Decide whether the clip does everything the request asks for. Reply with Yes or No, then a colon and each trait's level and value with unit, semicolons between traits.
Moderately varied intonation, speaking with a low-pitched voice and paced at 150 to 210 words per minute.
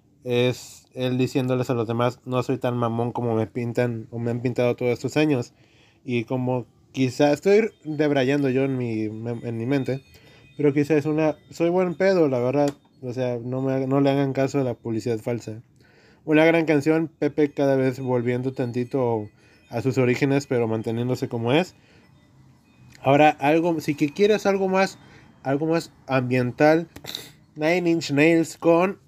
Yes: average, 3.7 semitones; low, 130 Hz; average, 165 wpm